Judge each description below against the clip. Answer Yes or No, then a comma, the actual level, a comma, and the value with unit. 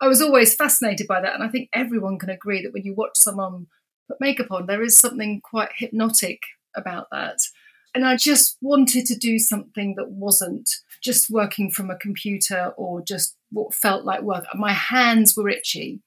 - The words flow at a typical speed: Yes, average, 190 wpm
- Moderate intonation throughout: Yes, average, 4.1 semitones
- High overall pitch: Yes, high, 220 Hz